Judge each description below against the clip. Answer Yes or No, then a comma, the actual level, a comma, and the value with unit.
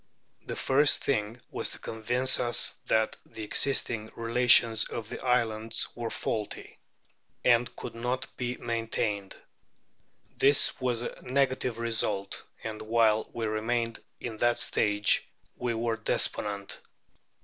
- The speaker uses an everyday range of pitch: No, narrow, 2.1 semitones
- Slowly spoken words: Yes, slow, 125 wpm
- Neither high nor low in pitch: No, low, 115 Hz